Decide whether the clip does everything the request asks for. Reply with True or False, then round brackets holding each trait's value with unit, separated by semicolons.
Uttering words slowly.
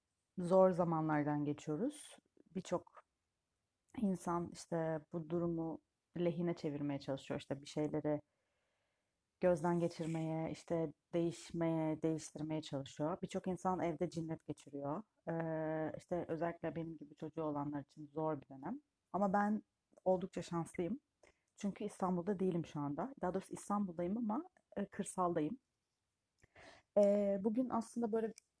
False (115 wpm)